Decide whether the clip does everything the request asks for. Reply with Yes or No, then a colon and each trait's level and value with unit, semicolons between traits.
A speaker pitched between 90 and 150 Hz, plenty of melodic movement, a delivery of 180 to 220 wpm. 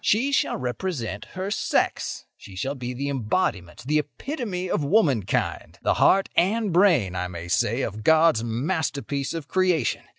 No: medium, 140 Hz; wide, 8.5 semitones; average, 145 wpm